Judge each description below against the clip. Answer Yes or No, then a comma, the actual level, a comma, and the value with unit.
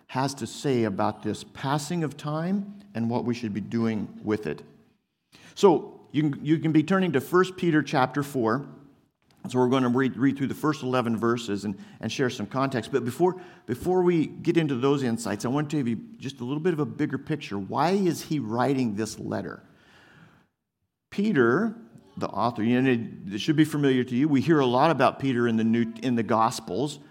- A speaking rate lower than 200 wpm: No, fast, 205 wpm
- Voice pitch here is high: No, low, 135 Hz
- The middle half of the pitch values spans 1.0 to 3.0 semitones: No, average, 4.9 semitones